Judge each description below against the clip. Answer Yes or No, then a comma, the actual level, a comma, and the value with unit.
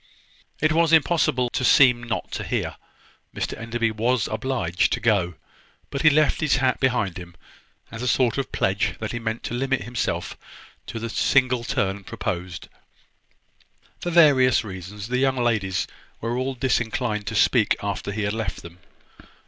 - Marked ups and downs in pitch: No, average, 4.1 semitones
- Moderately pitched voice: No, low, 120 Hz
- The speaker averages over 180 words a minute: No, average, 165 wpm